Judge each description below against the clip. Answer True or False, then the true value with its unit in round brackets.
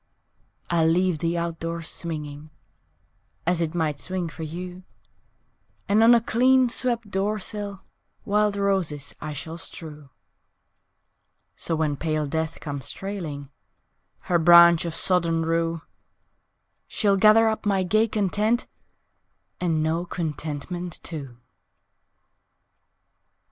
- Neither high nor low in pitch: True (170 Hz)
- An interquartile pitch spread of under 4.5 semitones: True (4.0 semitones)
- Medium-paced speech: False (115 wpm)